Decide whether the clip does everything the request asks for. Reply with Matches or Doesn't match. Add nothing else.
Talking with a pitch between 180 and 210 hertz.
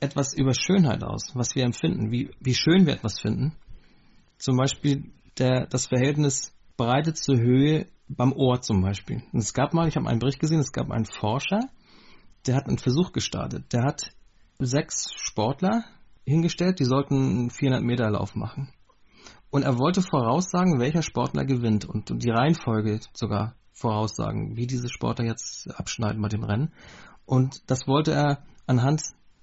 Doesn't match